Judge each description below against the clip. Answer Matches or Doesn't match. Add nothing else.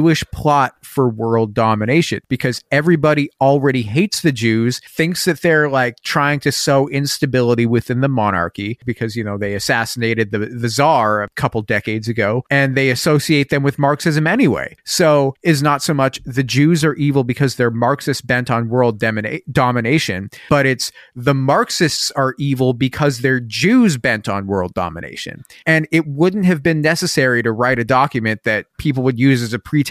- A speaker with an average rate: Matches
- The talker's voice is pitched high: Doesn't match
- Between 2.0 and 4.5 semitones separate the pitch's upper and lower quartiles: Matches